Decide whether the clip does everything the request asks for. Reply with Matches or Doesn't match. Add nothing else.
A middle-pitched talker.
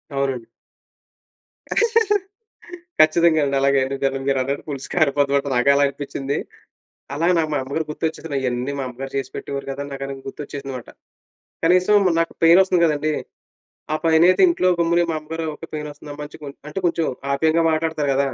Matches